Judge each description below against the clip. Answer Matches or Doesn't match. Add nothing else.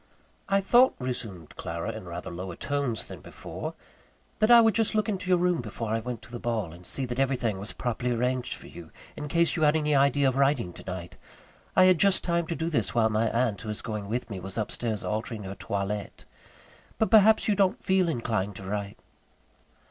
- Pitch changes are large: Matches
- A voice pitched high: Doesn't match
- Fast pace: Matches